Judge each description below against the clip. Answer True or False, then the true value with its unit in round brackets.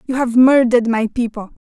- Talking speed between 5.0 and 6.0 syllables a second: True (5.8 syllables/s)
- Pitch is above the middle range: True (240 Hz)